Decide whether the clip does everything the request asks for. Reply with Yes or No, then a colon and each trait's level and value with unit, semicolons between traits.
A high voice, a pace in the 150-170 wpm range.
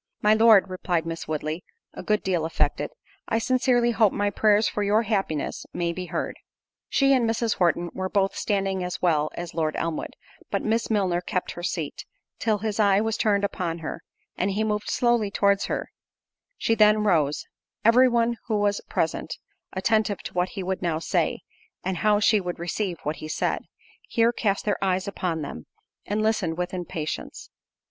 No: high, 195 Hz; average, 180 wpm